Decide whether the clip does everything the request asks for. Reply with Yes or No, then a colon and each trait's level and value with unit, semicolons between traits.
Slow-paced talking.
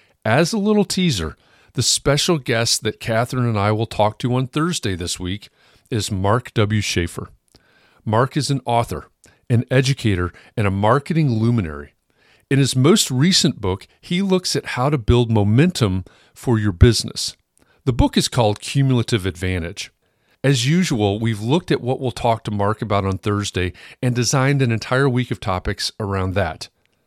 No: average, 165 wpm